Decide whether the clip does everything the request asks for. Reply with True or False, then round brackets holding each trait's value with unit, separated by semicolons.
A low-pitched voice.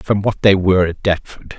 True (95 Hz)